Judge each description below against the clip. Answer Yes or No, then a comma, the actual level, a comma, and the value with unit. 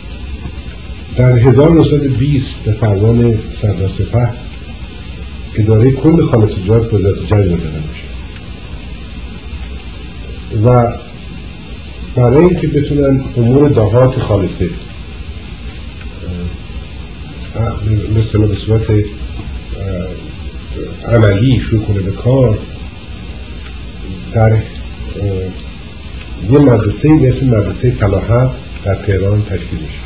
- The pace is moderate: No, slow, 75 wpm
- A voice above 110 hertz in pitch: No, very low, 95 Hz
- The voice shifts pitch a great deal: Yes, wide, 6.4 semitones